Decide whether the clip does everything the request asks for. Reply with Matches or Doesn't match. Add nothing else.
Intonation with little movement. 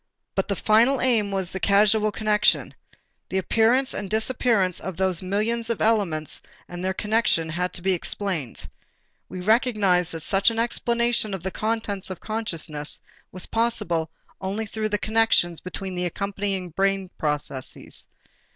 Doesn't match